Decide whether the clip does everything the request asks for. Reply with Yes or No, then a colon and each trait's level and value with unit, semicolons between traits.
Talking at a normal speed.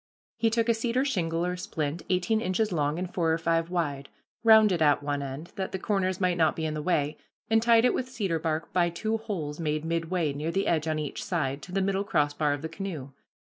No: fast, 230 wpm